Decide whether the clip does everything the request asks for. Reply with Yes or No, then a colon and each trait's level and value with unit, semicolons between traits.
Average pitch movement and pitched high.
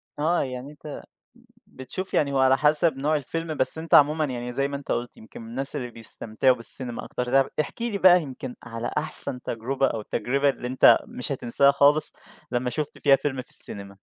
No: average, 3.2 semitones; low, 135 Hz